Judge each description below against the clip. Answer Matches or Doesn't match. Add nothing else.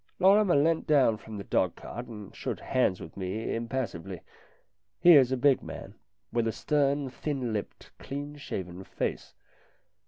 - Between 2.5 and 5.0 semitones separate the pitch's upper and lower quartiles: Doesn't match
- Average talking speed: Matches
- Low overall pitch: Matches